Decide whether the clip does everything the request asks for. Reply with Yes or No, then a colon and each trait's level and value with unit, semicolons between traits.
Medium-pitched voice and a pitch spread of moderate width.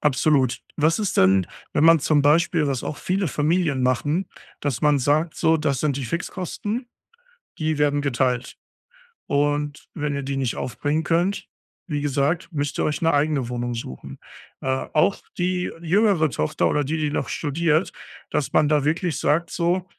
Yes: medium, 150 Hz; average, 3.1 semitones